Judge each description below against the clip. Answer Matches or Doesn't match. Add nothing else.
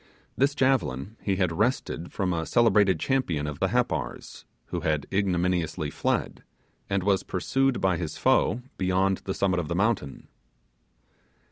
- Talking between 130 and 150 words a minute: Matches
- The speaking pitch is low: Matches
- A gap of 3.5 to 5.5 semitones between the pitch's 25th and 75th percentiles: Matches